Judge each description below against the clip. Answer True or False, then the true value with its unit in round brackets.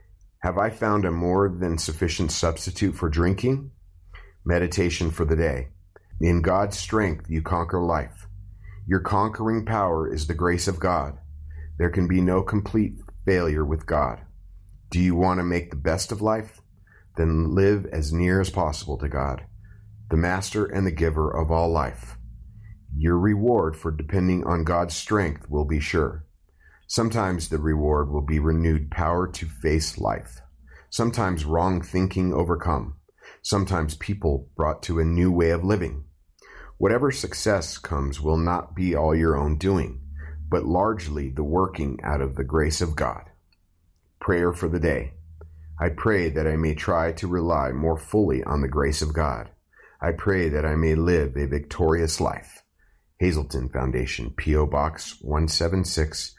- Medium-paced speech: True (155 wpm)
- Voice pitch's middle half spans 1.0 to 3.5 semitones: True (3.2 semitones)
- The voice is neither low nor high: False (85 Hz)